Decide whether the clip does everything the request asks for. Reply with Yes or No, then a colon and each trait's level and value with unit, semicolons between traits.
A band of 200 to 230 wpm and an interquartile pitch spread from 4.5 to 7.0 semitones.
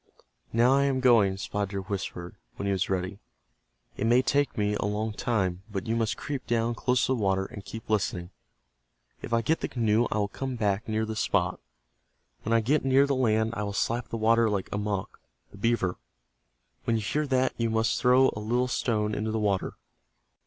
No: fast, 205 wpm; average, 3.0 semitones